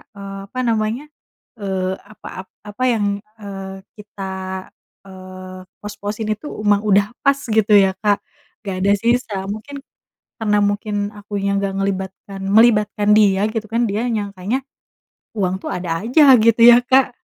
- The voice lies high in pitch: Yes, high, 205 Hz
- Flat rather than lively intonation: Yes, narrow, 2.2 semitones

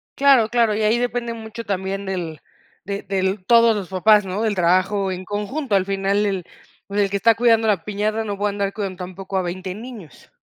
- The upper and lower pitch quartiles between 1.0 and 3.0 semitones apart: Yes, narrow, 2.6 semitones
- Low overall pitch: No, high, 200 Hz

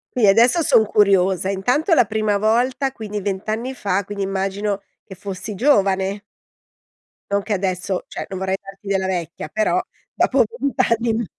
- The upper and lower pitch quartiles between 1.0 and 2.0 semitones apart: No, narrow, 2.5 semitones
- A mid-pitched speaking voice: No, high, 200 Hz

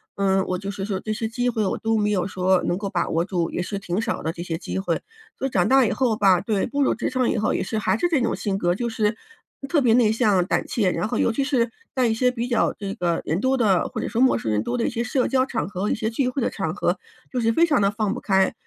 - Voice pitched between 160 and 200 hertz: No, high, 215 Hz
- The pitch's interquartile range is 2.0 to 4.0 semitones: No, average, 4.4 semitones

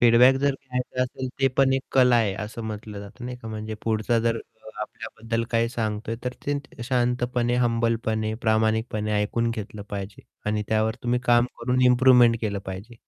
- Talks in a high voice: No, low, 115 Hz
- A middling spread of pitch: No, narrow, 2.2 semitones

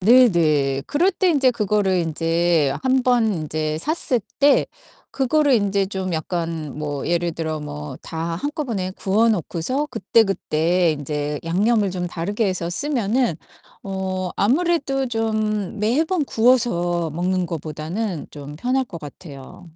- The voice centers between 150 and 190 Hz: Yes, medium, 185 Hz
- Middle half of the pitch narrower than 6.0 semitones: No, wide, 6.4 semitones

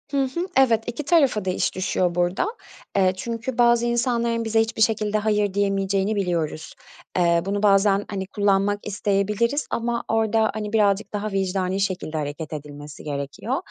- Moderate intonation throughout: Yes, average, 3.3 semitones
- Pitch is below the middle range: No, high, 205 Hz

